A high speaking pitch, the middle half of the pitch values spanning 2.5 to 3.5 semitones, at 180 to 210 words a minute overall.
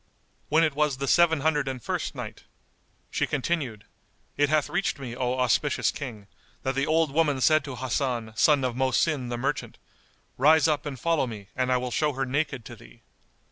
No: low, 135 Hz; average, 3.2 semitones; average, 190 wpm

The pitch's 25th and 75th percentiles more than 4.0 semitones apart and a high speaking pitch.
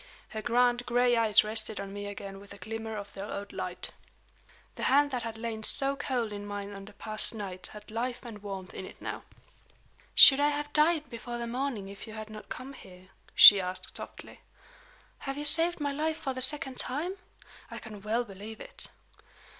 Yes: average, 4.6 semitones; high, 225 Hz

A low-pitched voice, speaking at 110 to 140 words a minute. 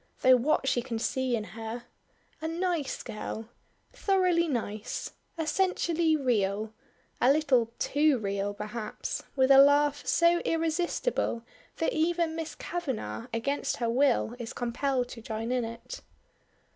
No: very high, 260 Hz; slow, 135 wpm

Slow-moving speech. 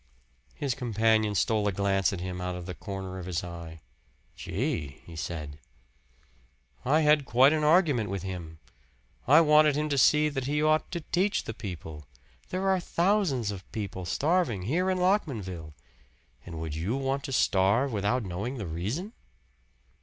No: average, 165 wpm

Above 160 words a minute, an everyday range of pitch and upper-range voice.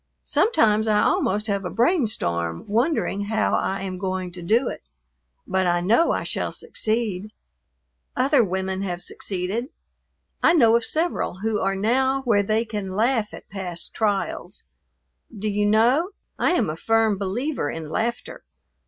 No: average, 155 wpm; average, 3.7 semitones; high, 210 Hz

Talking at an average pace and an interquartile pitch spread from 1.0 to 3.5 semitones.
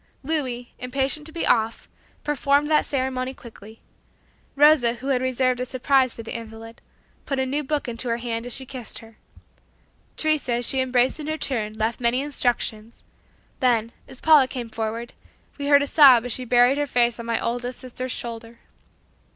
Yes: average, 185 wpm; average, 2.8 semitones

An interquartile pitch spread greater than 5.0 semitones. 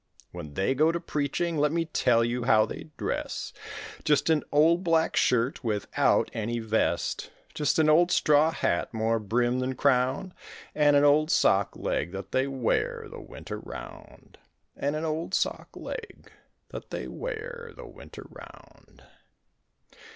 Yes: wide, 5.5 semitones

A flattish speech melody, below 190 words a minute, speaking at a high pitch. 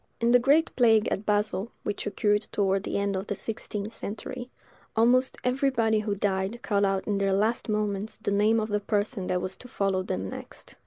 No: narrow, 2.3 semitones; average, 200 wpm; high, 210 Hz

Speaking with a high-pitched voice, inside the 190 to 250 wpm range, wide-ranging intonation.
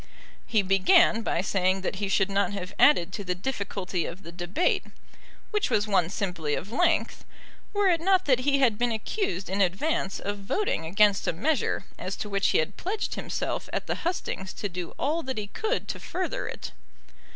Yes: high, 205 Hz; average, 195 wpm; wide, 6.8 semitones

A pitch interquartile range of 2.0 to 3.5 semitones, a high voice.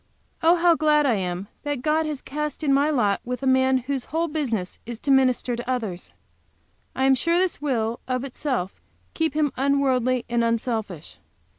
No: average, 3.9 semitones; very high, 265 Hz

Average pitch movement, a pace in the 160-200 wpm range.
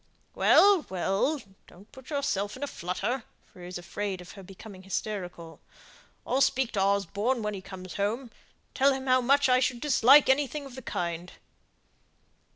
No: wide, 5.8 semitones; average, 170 wpm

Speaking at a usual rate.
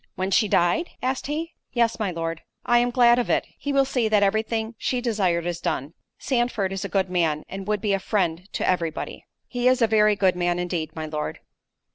No: fast, 215 wpm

